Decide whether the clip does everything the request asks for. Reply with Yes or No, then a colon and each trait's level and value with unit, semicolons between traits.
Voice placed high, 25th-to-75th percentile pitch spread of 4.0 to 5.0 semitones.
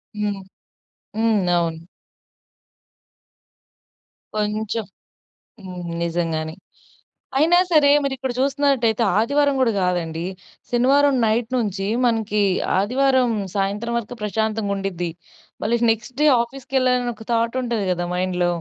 Yes: high, 220 Hz; average, 4.6 semitones